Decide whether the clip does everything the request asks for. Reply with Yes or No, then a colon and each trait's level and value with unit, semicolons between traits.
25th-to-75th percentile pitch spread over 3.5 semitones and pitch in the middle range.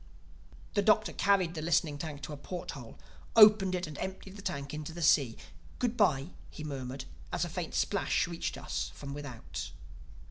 Yes: average, 5.1 semitones; medium, 155 Hz